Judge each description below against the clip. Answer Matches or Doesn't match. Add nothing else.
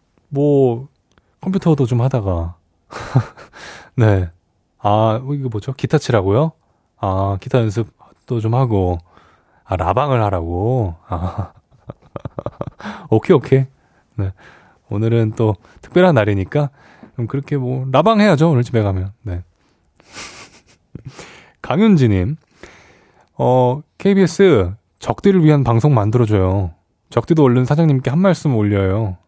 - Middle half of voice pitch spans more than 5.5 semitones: Matches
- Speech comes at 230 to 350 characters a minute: Doesn't match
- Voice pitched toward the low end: Matches